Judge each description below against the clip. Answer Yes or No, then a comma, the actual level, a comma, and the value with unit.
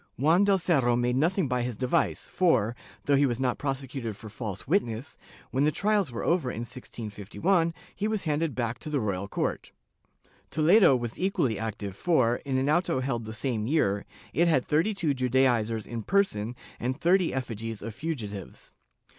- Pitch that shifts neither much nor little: No, wide, 6.1 semitones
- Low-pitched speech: Yes, low, 130 Hz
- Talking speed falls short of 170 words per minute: No, average, 175 wpm